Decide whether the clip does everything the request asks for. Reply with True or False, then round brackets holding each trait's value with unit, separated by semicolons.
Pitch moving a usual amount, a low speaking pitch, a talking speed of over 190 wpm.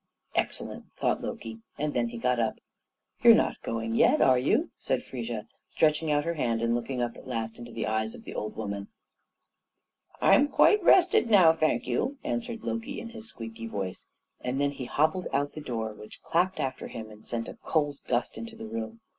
False (5.7 semitones; 125 Hz; 200 wpm)